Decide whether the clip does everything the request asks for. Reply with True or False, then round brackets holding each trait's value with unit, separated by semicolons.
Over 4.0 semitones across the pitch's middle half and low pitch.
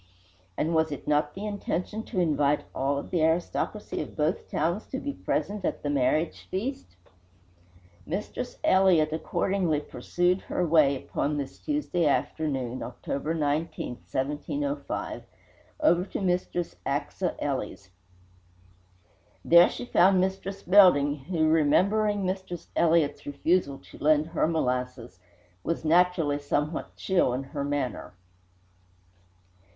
False (4.4 semitones; 160 Hz)